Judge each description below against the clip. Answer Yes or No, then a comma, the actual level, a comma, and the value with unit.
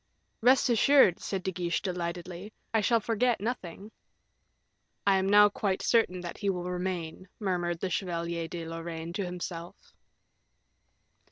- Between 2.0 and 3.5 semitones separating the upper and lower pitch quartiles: Yes, average, 3.1 semitones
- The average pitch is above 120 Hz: Yes, medium, 185 Hz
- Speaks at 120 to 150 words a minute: Yes, average, 140 wpm